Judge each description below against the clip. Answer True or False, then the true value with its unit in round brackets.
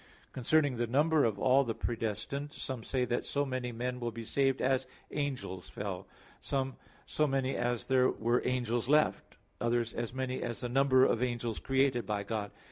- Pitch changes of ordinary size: False (2.3 semitones)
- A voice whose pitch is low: True (125 Hz)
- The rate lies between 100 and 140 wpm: False (180 wpm)